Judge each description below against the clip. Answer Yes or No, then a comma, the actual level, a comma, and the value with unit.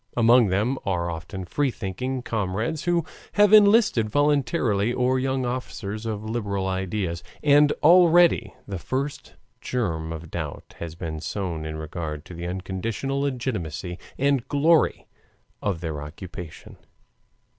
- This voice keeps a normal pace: No, slow, 130 wpm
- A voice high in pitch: No, low, 110 Hz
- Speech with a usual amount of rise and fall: No, wide, 7.4 semitones